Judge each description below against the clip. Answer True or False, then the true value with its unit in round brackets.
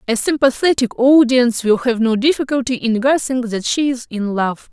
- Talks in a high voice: True (245 Hz)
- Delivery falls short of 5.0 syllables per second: False (5.2 syllables/s)